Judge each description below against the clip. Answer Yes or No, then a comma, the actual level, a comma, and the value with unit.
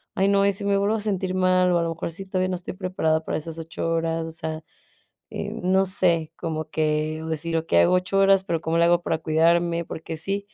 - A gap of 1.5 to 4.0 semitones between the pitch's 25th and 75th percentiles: Yes, average, 2.7 semitones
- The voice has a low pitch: No, medium, 170 Hz